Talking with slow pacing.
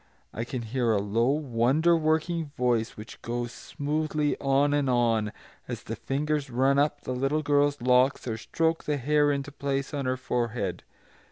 No: average, 170 wpm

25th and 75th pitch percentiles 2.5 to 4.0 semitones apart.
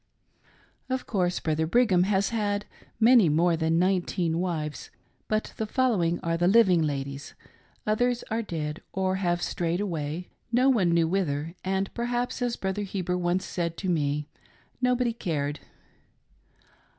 No: average, 4.5 semitones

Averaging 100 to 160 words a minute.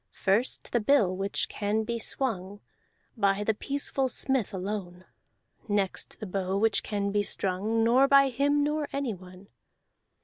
Yes: average, 140 wpm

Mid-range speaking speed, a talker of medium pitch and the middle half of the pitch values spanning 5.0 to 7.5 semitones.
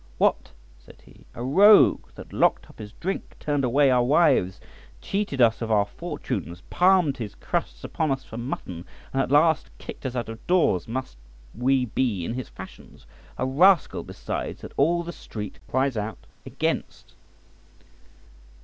No: average, 160 wpm; low, 130 Hz; wide, 5.6 semitones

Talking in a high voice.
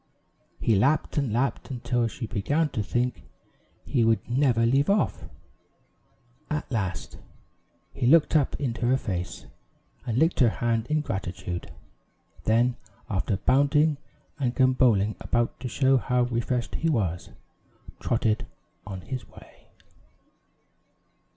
No: low, 120 Hz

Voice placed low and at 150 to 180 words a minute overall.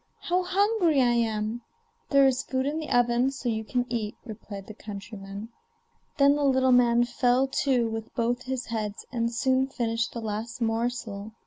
No: high, 240 Hz; average, 175 wpm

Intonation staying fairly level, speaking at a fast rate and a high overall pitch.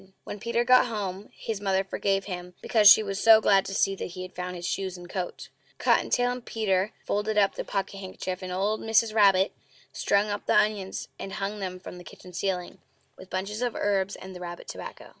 Yes: narrow, 2.3 semitones; fast, 220 wpm; high, 195 Hz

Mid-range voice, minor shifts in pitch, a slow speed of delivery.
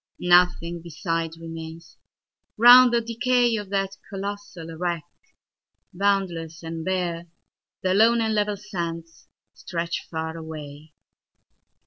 No: medium, 175 Hz; average, 3.7 semitones; slow, 95 wpm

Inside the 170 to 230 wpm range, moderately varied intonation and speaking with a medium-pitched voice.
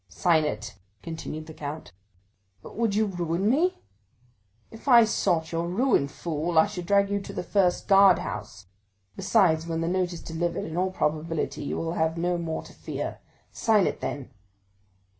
Yes: average, 175 wpm; average, 3.7 semitones; medium, 170 Hz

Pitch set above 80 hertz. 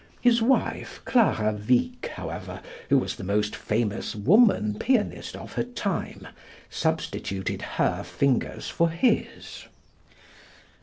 Yes: medium, 140 Hz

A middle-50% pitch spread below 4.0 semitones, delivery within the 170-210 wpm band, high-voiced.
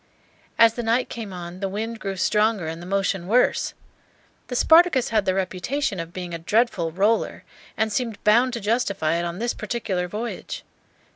No: average, 4.3 semitones; average, 180 wpm; high, 210 Hz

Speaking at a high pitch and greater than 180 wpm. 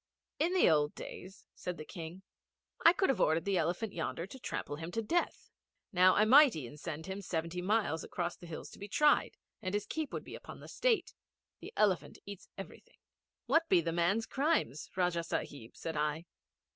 No: medium, 180 Hz; average, 195 wpm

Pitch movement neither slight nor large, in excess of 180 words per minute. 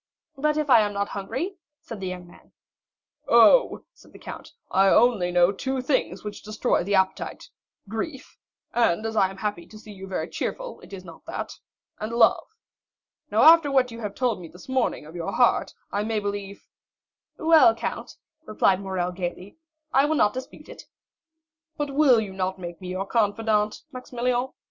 No: average, 5.0 semitones; average, 170 wpm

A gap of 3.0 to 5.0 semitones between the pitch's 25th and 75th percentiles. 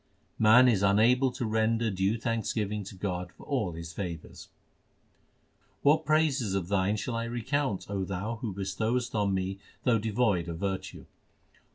Yes: average, 3.7 semitones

